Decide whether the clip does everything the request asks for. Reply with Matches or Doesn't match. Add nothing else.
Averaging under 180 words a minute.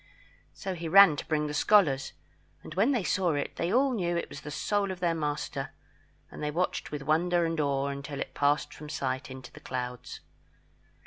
Doesn't match